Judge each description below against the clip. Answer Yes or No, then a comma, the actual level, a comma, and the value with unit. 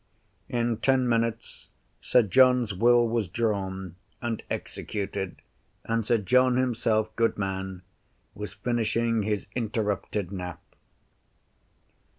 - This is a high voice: No, low, 110 Hz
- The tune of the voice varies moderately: Yes, average, 3.1 semitones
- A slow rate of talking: Yes, slow, 105 wpm